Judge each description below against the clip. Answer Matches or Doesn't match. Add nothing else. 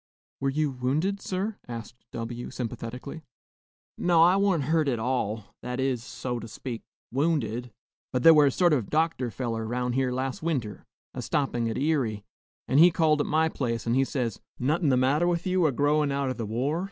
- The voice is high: Doesn't match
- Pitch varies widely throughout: Doesn't match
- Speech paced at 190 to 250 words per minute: Matches